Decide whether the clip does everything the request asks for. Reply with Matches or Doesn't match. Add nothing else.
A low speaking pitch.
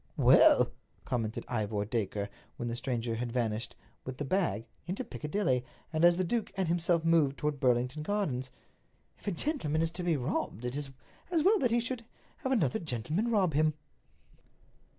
Doesn't match